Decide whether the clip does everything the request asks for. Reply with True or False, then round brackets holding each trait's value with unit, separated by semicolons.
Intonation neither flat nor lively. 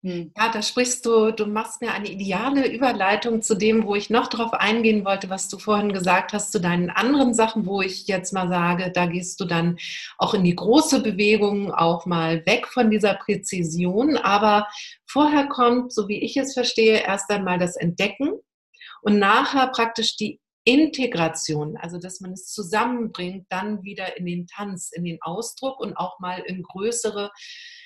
True (3.8 semitones)